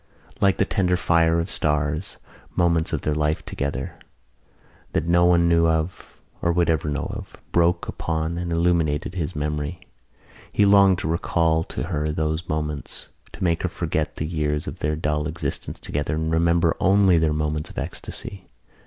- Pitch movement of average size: No, narrow, 2.1 semitones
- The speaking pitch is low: Yes, very low, 80 Hz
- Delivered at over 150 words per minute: Yes, average, 170 wpm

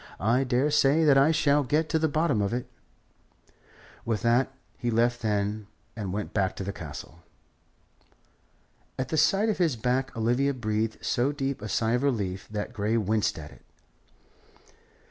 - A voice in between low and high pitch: No, low, 120 Hz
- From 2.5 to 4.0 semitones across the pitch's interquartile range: No, average, 4.7 semitones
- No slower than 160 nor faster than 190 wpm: Yes, average, 165 wpm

